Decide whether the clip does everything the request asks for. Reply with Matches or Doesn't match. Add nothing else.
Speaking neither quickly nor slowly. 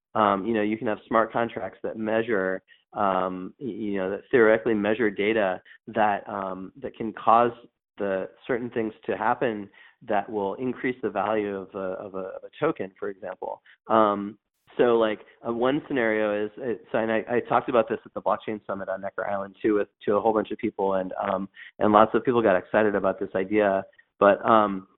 Matches